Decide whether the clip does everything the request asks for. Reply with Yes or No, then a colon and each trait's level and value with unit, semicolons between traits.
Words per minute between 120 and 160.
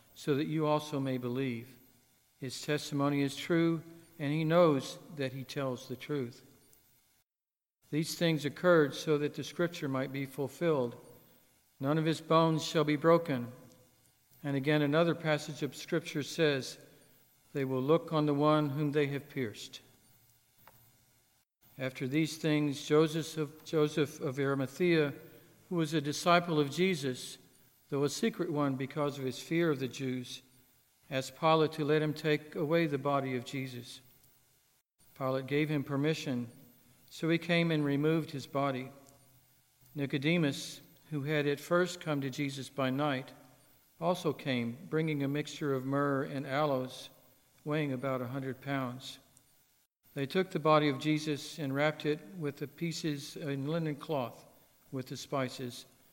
Yes: average, 150 wpm